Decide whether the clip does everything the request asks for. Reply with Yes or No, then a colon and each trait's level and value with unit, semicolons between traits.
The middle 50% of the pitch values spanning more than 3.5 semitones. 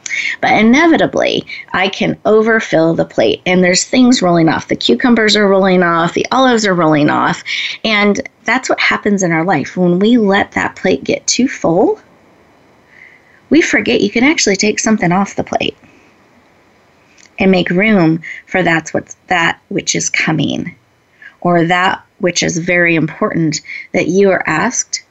Yes: average, 4.0 semitones